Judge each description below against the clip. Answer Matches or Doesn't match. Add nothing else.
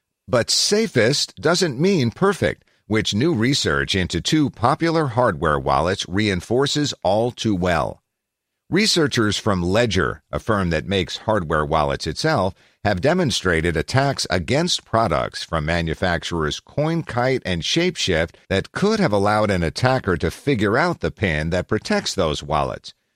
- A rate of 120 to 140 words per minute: Matches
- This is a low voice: Matches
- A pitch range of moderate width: Doesn't match